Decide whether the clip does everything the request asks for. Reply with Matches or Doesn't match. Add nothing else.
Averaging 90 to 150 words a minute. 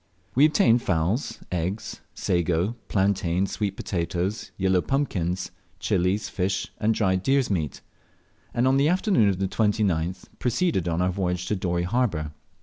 Matches